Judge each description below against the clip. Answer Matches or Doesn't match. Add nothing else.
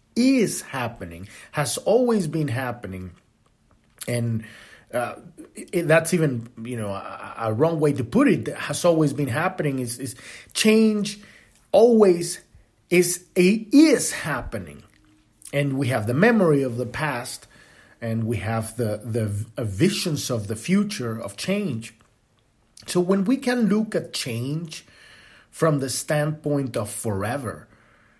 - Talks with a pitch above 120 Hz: Matches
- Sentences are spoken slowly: Matches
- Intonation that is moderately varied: Doesn't match